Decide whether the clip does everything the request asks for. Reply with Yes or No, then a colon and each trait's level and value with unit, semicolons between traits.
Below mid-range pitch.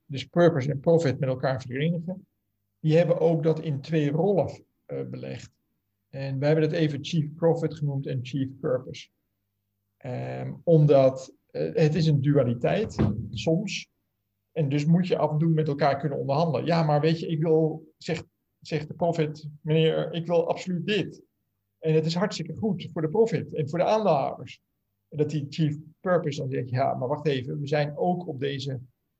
No: medium, 150 Hz